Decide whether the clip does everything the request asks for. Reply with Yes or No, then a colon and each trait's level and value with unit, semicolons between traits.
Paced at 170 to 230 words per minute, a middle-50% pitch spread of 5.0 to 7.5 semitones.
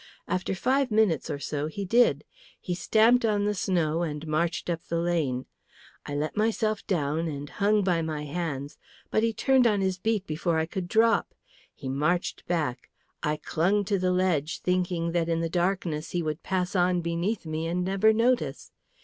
No: average, 185 wpm; average, 4.3 semitones